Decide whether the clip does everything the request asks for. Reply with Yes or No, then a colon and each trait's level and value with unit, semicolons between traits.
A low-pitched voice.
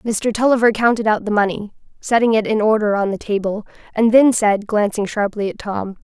No: high, 215 Hz